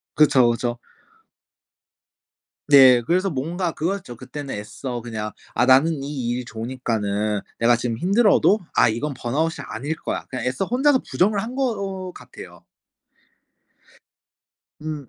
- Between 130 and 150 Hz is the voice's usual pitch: Yes, low, 135 Hz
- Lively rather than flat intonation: Yes, wide, 6.5 semitones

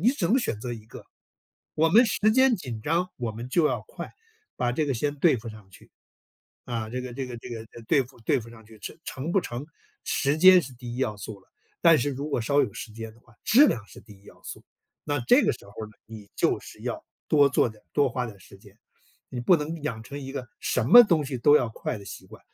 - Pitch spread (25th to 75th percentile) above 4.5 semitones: Yes, average, 5.3 semitones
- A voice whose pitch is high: No, low, 125 Hz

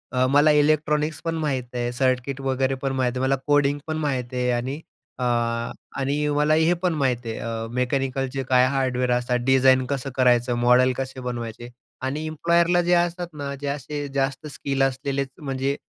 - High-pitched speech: No, low, 135 Hz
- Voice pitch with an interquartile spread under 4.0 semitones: Yes, narrow, 2.6 semitones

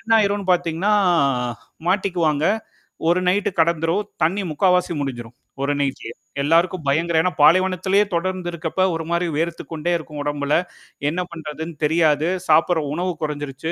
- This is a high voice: No, medium, 165 Hz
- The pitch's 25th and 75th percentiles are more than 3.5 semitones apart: No, average, 3.1 semitones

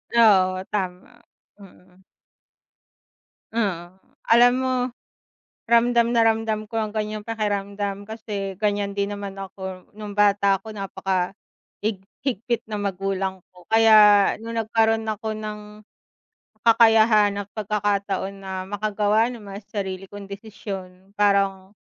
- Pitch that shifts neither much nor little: No, narrow, 2.0 semitones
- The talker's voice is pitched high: Yes, high, 205 Hz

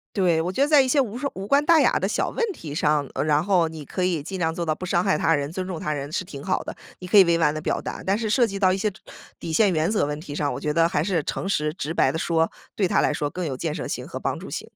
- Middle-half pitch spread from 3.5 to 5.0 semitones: Yes, average, 4.2 semitones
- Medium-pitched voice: Yes, medium, 170 Hz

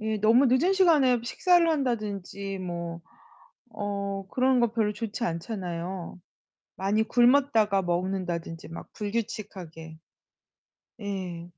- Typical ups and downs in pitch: Yes, average, 4.8 semitones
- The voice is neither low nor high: No, high, 205 Hz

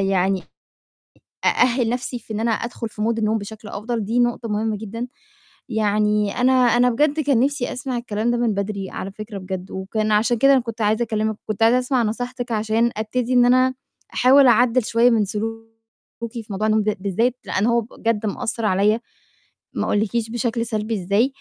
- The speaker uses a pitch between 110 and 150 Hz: No, high, 225 Hz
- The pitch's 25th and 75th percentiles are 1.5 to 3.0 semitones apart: Yes, narrow, 2.4 semitones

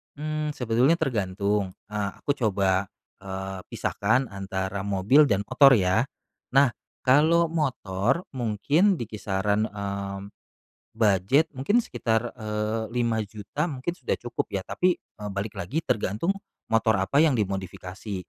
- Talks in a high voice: No, low, 110 Hz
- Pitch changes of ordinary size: No, wide, 5.7 semitones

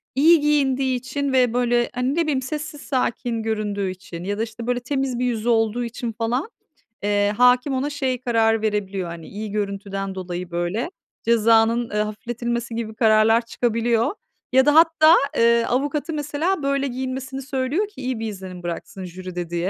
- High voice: Yes, high, 235 Hz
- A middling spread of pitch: Yes, average, 4.0 semitones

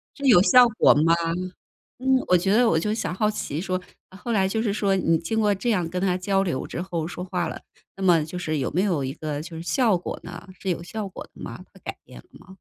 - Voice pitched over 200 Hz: No, medium, 185 Hz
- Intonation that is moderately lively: Yes, average, 3.8 semitones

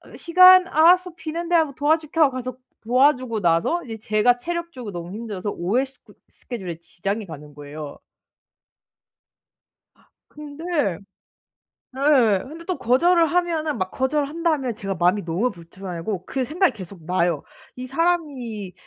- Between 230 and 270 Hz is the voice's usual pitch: Yes, very high, 255 Hz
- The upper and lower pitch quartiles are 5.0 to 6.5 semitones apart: No, wide, 8.7 semitones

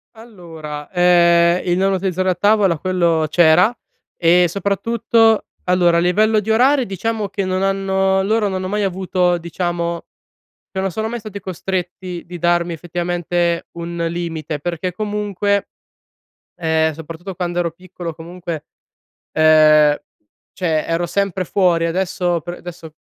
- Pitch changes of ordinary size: No, narrow, 2.3 semitones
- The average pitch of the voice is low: No, medium, 180 Hz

